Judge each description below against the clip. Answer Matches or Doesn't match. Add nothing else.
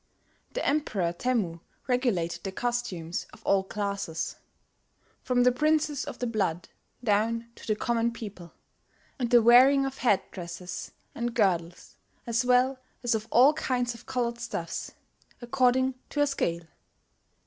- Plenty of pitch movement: Doesn't match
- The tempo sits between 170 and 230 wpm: Doesn't match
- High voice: Matches